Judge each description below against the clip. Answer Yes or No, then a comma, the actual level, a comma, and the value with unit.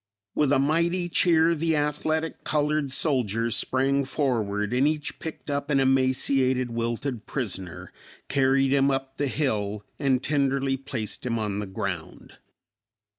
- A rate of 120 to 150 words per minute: Yes, slow, 135 wpm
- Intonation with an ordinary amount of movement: Yes, average, 3.8 semitones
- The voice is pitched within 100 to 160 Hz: Yes, low, 135 Hz